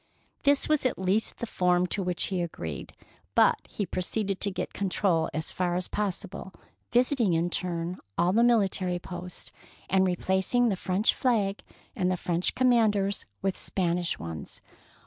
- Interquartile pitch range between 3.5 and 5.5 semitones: No, average, 2.8 semitones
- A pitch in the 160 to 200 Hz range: Yes, high, 190 Hz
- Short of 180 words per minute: Yes, average, 165 wpm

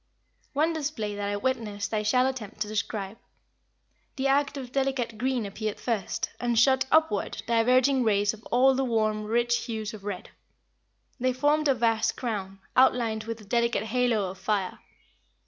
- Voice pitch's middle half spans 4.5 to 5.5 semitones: No, average, 3.5 semitones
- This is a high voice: Yes, high, 230 Hz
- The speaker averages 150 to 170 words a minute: Yes, average, 165 wpm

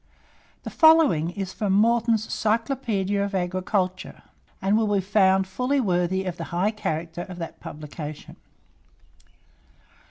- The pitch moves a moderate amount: Yes, average, 3.5 semitones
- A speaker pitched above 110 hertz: Yes, high, 190 Hz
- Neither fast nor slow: No, slow, 125 wpm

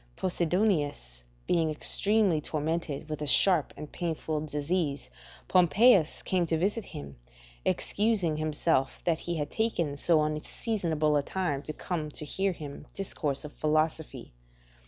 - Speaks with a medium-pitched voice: Yes, medium, 155 Hz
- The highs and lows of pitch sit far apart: No, average, 3.4 semitones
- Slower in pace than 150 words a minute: Yes, slow, 135 wpm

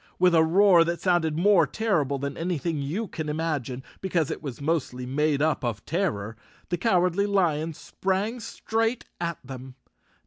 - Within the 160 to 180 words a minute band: Yes, average, 165 wpm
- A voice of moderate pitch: Yes, medium, 165 Hz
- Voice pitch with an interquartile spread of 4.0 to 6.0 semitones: Yes, average, 4.7 semitones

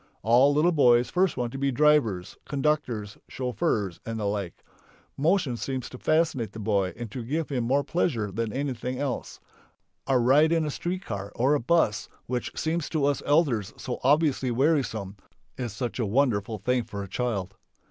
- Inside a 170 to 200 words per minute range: Yes, average, 180 wpm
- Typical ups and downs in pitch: Yes, average, 4.8 semitones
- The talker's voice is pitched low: Yes, low, 125 Hz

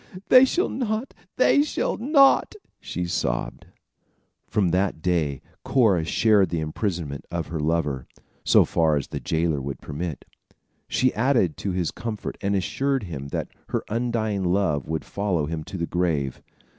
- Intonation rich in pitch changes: Yes, wide, 5.9 semitones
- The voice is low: Yes, very low, 90 Hz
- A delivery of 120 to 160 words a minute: Yes, average, 155 wpm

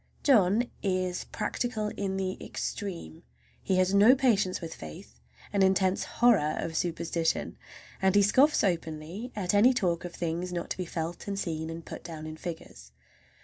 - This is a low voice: No, medium, 185 Hz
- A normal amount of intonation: Yes, average, 3.5 semitones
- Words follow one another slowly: No, average, 165 wpm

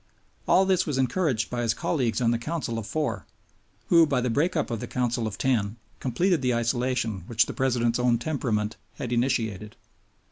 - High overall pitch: No, low, 125 Hz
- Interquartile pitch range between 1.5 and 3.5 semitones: Yes, average, 3.2 semitones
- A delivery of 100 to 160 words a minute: No, average, 185 wpm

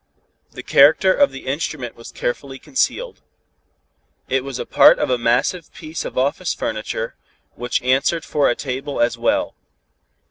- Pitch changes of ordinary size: Yes, average, 4.2 semitones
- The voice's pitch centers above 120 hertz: Yes, low, 135 Hz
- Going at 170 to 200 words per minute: No, average, 150 wpm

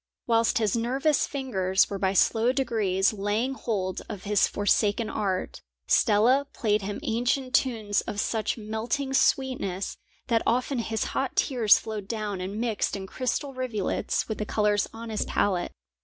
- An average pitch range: Yes, average, 3.3 semitones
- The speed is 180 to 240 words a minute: No, average, 155 wpm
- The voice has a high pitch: Yes, high, 220 Hz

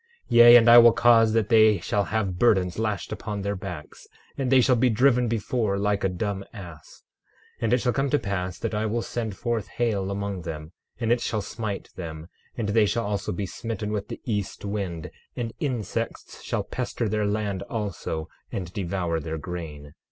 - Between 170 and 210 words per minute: Yes, average, 195 wpm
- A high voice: No, low, 105 Hz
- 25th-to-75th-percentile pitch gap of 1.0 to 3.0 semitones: No, average, 3.7 semitones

